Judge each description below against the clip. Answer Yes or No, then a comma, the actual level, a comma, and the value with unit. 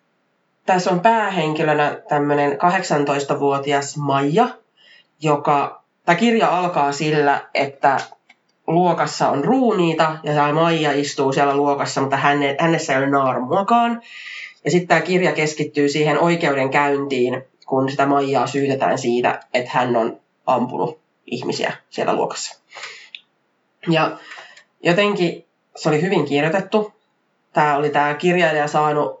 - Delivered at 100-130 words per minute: Yes, average, 115 wpm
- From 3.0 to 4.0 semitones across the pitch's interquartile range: Yes, average, 3.5 semitones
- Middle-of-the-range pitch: Yes, medium, 150 Hz